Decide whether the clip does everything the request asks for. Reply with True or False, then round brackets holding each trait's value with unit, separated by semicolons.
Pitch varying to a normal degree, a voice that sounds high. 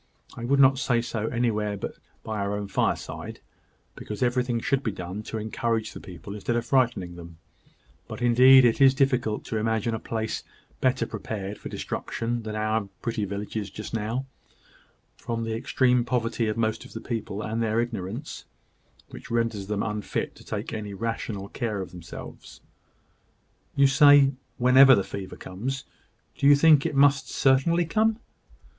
False (3.5 semitones; 115 Hz)